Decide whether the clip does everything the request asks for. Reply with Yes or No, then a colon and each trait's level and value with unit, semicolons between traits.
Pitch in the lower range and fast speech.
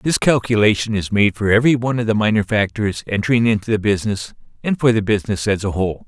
Yes: low, 110 Hz; fast, 215 wpm